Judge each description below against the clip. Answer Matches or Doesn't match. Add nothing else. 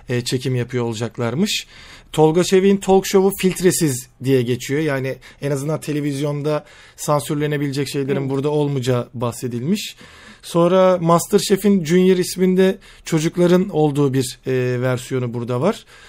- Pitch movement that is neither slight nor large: Doesn't match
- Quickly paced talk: Doesn't match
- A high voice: Doesn't match